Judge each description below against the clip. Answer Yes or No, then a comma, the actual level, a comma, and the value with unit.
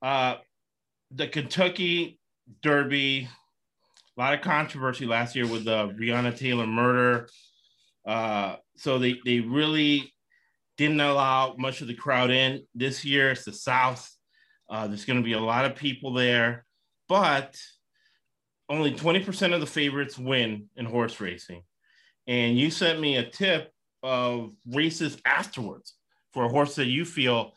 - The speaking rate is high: No, average, 145 wpm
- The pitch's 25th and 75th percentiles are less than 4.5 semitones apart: Yes, average, 3.4 semitones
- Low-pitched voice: Yes, low, 130 Hz